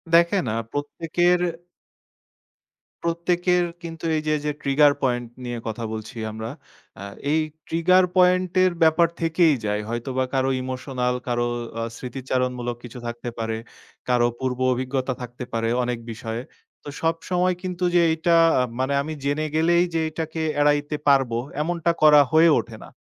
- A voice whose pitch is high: No, medium, 145 Hz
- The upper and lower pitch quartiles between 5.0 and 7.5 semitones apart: Yes, wide, 5.4 semitones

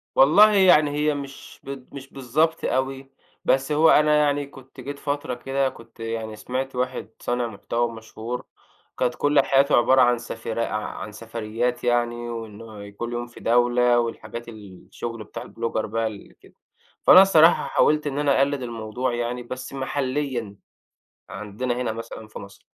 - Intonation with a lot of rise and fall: No, average, 3.2 semitones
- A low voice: Yes, low, 125 Hz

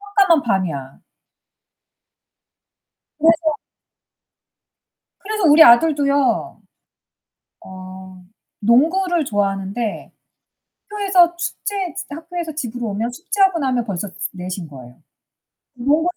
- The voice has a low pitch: No, very high, 265 Hz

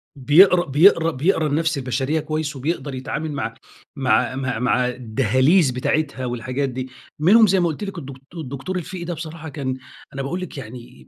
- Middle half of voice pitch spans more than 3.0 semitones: Yes, average, 4.1 semitones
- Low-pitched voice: No, medium, 145 Hz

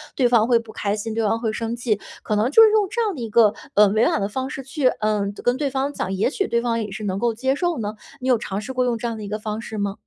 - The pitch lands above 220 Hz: Yes, high, 230 Hz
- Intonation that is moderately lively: Yes, average, 3.5 semitones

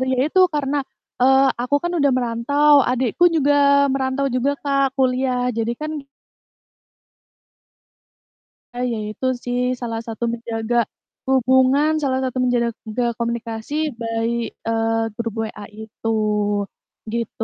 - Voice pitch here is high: Yes, very high, 255 Hz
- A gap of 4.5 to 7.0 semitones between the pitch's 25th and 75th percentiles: No, average, 3.4 semitones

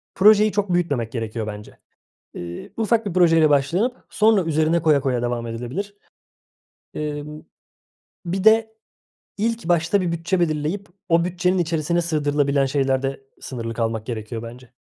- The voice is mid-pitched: Yes, medium, 155 Hz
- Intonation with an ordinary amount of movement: No, wide, 6.2 semitones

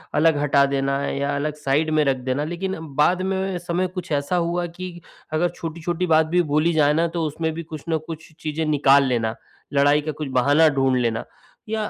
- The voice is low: No, medium, 155 Hz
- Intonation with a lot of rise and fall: No, average, 3.3 semitones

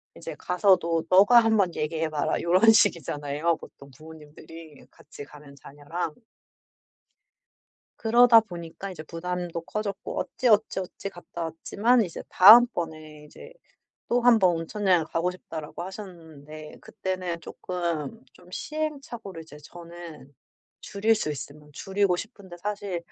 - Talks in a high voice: No, medium, 175 Hz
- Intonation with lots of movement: No, average, 4.3 semitones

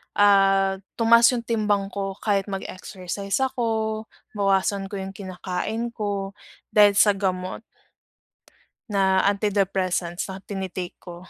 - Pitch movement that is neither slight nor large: No, narrow, 1.7 semitones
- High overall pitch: Yes, high, 195 Hz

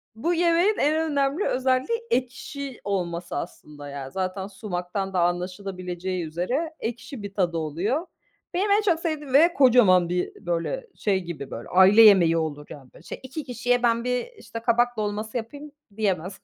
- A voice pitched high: Yes, high, 215 Hz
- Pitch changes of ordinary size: No, wide, 7.5 semitones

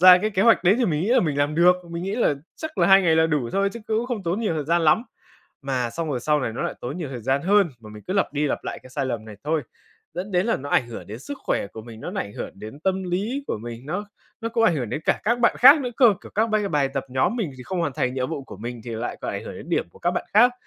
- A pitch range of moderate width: No, wide, 7.4 semitones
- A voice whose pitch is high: No, medium, 165 Hz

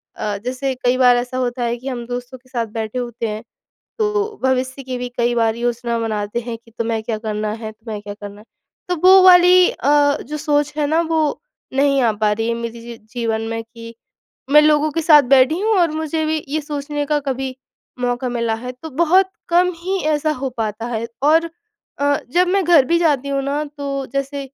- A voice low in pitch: No, very high, 260 Hz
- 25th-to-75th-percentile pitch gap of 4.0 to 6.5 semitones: Yes, average, 4.4 semitones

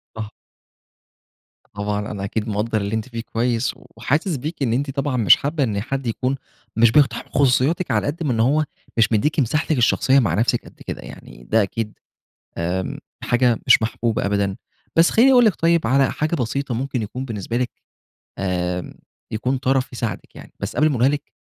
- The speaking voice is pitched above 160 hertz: No, low, 120 Hz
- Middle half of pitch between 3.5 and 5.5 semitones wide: Yes, average, 4.2 semitones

